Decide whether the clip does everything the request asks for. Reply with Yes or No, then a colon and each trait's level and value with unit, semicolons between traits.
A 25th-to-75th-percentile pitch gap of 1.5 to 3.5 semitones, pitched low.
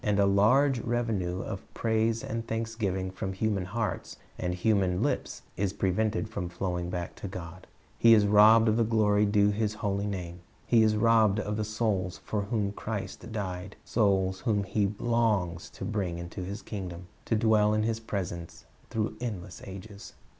Yes: average, 2.9 semitones; low, 105 Hz